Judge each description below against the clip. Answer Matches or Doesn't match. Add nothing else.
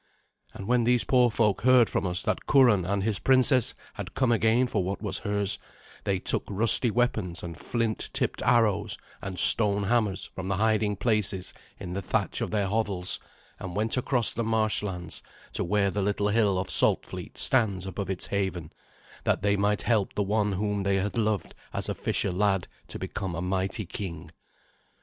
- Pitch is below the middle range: Matches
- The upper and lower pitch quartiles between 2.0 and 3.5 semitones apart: Matches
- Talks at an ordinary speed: Matches